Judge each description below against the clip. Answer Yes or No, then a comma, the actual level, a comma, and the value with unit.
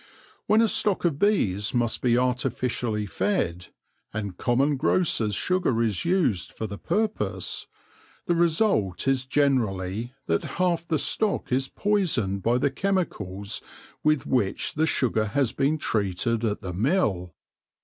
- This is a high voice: No, low, 125 Hz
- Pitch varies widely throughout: Yes, wide, 8.4 semitones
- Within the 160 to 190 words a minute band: No, average, 140 wpm